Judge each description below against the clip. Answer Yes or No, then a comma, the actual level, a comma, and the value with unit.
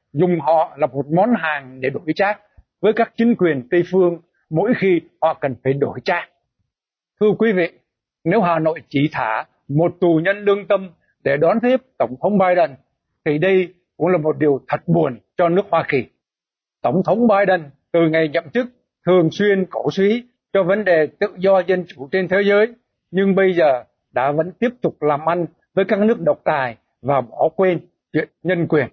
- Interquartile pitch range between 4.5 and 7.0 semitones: No, average, 3.8 semitones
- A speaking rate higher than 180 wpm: Yes, average, 195 wpm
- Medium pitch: Yes, medium, 175 Hz